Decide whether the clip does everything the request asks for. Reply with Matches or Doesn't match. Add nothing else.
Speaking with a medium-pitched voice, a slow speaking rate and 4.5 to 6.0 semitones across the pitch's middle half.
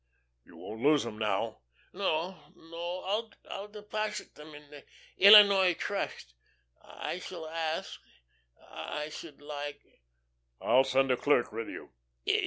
Matches